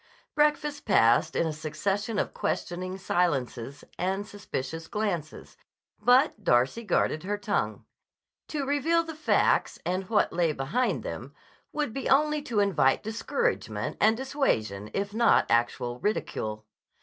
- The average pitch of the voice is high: Yes, high, 200 Hz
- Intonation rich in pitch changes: Yes, wide, 8.8 semitones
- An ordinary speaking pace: No, slow, 130 wpm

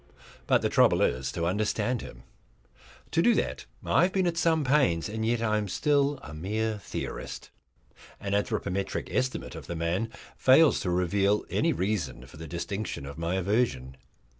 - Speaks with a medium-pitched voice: No, low, 100 Hz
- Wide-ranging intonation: Yes, wide, 6.9 semitones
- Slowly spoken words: No, average, 170 wpm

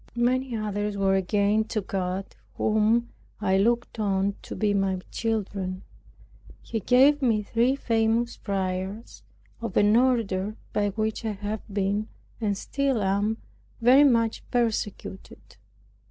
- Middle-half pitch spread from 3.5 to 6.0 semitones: No, average, 2.8 semitones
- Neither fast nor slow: No, slow, 125 wpm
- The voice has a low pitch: No, high, 215 Hz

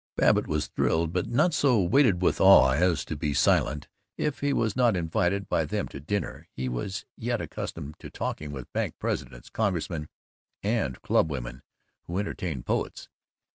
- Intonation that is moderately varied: No, wide, 6.7 semitones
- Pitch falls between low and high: No, very low, 90 Hz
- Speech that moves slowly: No, average, 165 wpm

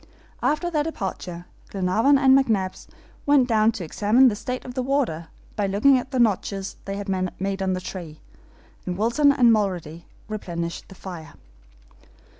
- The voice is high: Yes, high, 205 Hz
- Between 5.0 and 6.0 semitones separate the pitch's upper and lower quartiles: Yes, wide, 5.6 semitones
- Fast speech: No, average, 160 wpm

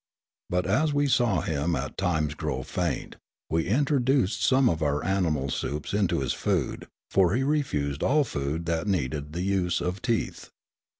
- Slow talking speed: No, average, 170 wpm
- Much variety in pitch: Yes, wide, 7.8 semitones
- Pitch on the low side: Yes, very low, 90 Hz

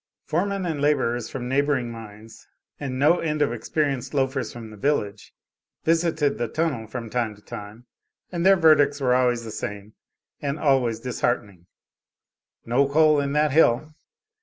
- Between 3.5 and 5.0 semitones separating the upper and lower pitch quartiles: Yes, average, 4.4 semitones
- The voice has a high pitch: No, low, 135 Hz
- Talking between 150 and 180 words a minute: Yes, average, 155 wpm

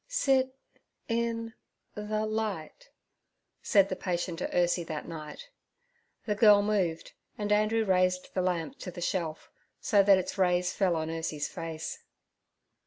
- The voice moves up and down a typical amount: Yes, average, 4.0 semitones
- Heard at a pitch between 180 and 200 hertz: Yes, high, 190 Hz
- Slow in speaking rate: Yes, slow, 125 wpm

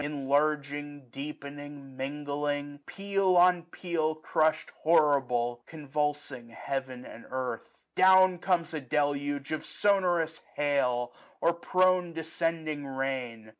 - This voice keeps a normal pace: No, slow, 100 wpm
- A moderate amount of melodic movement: Yes, average, 3.3 semitones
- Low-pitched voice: No, medium, 145 Hz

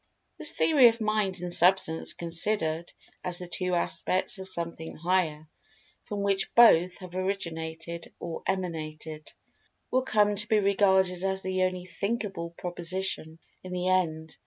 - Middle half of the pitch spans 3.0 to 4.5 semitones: No, narrow, 2.6 semitones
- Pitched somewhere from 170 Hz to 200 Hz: Yes, medium, 185 Hz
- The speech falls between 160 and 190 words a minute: No, average, 140 wpm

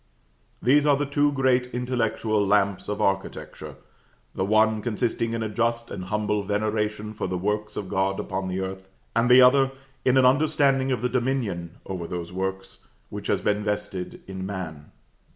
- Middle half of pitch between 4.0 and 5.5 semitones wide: Yes, average, 4.5 semitones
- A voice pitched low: Yes, low, 105 Hz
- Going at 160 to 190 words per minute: Yes, average, 170 wpm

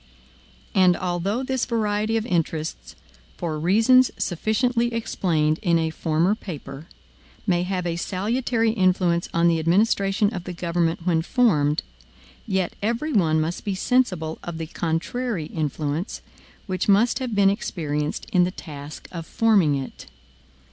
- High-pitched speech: No, medium, 180 Hz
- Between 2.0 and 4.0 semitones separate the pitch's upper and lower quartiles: No, average, 5.0 semitones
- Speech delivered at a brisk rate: No, average, 140 wpm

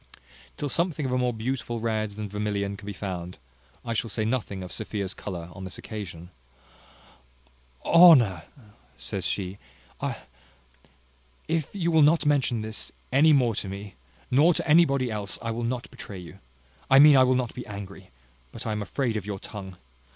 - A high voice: No, low, 110 Hz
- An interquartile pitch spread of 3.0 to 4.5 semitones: No, average, 4.9 semitones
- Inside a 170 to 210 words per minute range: Yes, average, 180 wpm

